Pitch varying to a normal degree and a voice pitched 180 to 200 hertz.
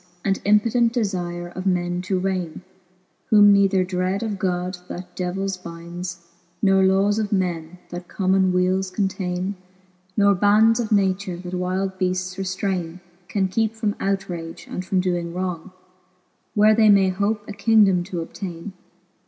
No: narrow, 2.0 semitones; high, 190 Hz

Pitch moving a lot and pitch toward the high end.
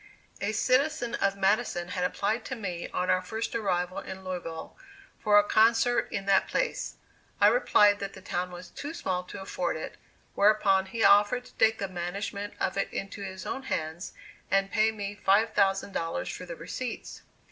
No: average, 3.1 semitones; high, 200 Hz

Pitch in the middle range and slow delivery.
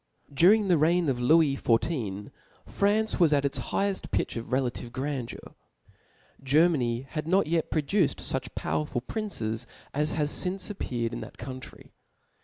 No: medium, 145 Hz; average, 145 wpm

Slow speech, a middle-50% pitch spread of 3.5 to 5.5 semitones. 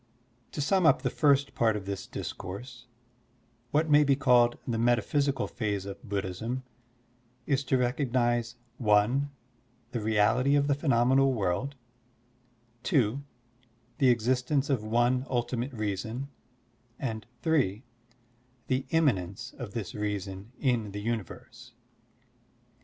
Yes: slow, 125 wpm; average, 4.3 semitones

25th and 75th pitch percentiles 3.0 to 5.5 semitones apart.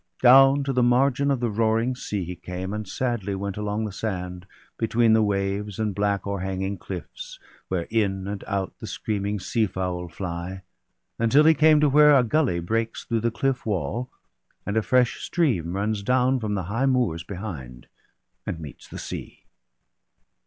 Yes: average, 4.5 semitones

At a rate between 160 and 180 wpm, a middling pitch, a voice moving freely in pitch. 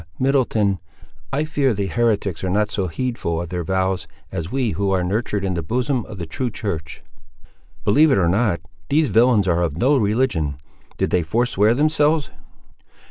No: average, 170 wpm; low, 105 Hz; wide, 5.9 semitones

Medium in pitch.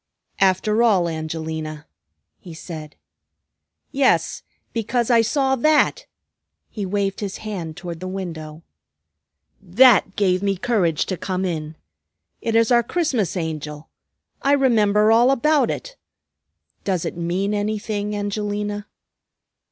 No: high, 200 Hz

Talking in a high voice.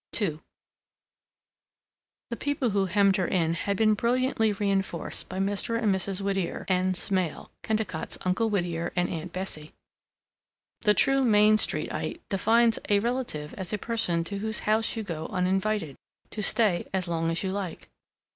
Yes: high, 195 Hz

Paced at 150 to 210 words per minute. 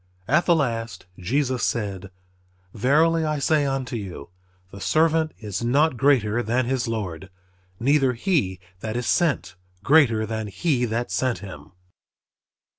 No: slow, 135 wpm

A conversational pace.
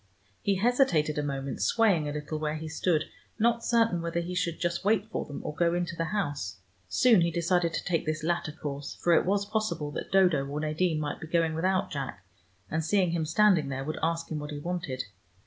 No: fast, 215 wpm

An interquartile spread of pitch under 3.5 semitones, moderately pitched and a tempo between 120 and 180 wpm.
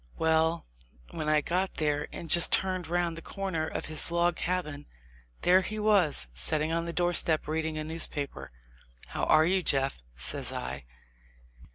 Yes: narrow, 2.5 semitones; medium, 160 Hz; average, 165 wpm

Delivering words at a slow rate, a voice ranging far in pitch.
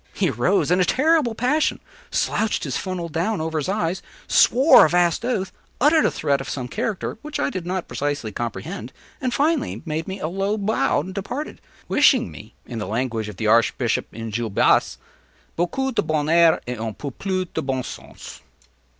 No: average, 185 wpm; wide, 8.8 semitones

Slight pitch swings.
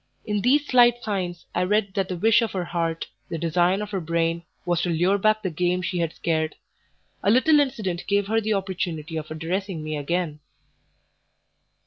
No: average, 3.8 semitones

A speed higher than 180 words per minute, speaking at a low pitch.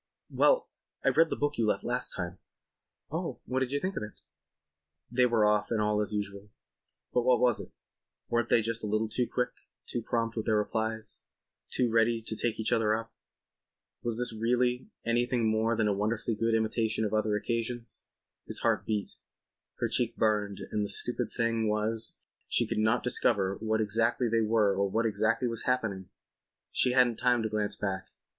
Yes: average, 190 wpm; low, 110 Hz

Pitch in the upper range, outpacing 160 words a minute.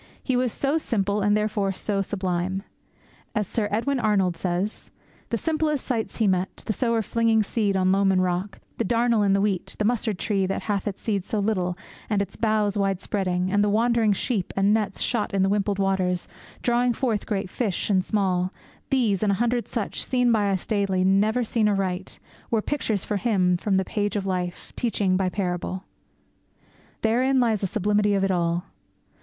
Yes: high, 205 Hz; average, 190 wpm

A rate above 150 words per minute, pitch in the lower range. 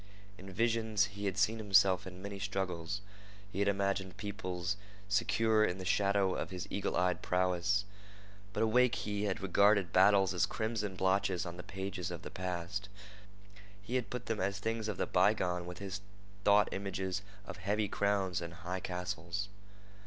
Yes: average, 165 wpm; low, 100 Hz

